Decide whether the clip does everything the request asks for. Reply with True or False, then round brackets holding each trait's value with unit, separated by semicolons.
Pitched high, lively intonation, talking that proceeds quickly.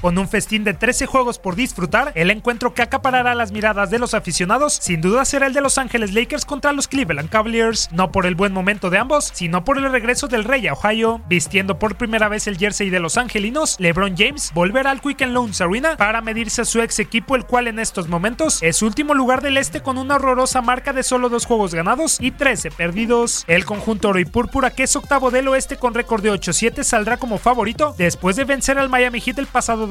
False (230 Hz; 4.4 semitones; 230 wpm)